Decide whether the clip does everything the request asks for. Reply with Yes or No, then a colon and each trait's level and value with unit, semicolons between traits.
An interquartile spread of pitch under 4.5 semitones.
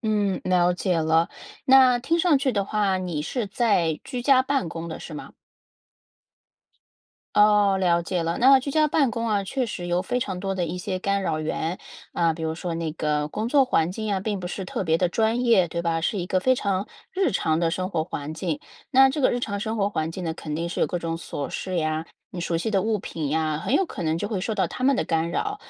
No: wide, 5.6 semitones